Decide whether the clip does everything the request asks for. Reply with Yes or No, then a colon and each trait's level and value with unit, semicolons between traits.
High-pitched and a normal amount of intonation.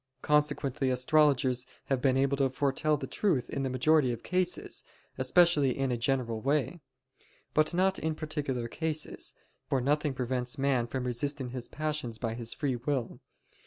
No: low, 135 Hz; average, 3.3 semitones